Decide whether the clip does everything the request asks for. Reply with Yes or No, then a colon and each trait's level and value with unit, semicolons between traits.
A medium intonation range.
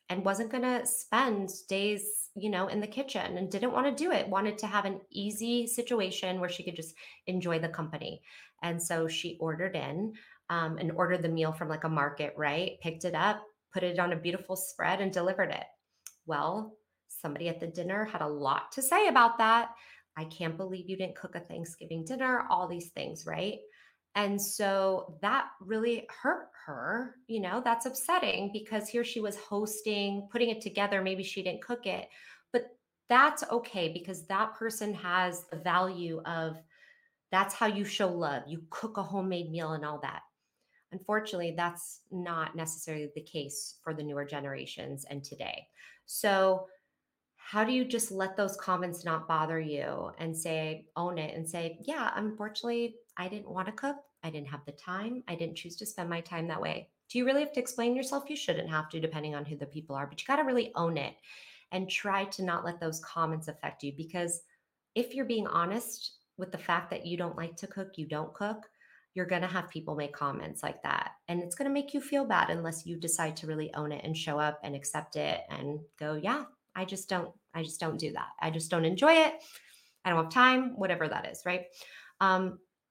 Yes: average, 4.8 semitones